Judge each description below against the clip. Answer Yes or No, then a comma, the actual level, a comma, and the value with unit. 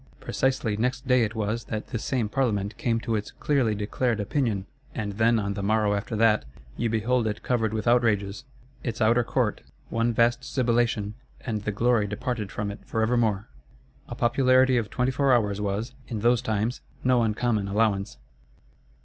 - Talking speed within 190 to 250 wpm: No, average, 175 wpm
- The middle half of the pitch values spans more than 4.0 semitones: No, narrow, 2.6 semitones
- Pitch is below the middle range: Yes, low, 115 Hz